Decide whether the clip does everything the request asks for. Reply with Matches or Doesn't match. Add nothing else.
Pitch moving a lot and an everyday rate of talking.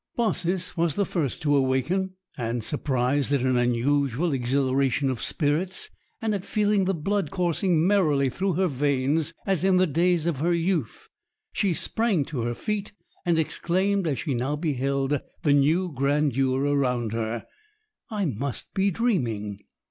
Matches